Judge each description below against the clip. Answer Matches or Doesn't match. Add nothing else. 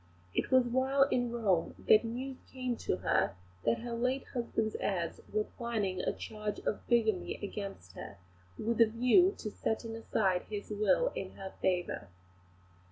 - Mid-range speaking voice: Doesn't match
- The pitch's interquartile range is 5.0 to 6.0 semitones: Doesn't match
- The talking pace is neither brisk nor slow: Matches